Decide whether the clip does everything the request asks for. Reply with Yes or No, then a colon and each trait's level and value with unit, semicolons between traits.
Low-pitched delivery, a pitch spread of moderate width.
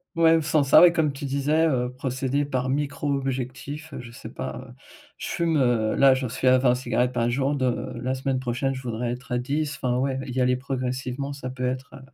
No: low, 130 Hz; narrow, 2.0 semitones